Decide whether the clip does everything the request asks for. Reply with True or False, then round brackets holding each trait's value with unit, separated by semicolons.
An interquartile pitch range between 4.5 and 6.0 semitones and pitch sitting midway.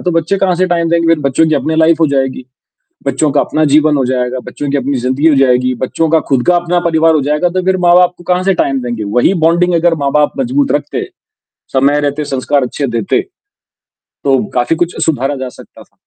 False (4.0 semitones; 150 Hz)